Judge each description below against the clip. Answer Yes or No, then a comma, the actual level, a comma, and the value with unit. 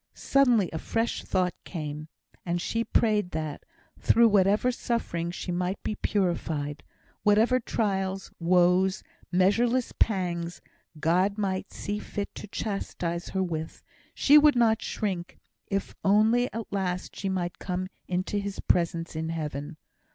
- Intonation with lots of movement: No, average, 3.5 semitones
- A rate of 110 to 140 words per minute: Yes, slow, 135 wpm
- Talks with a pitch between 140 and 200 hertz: Yes, high, 190 Hz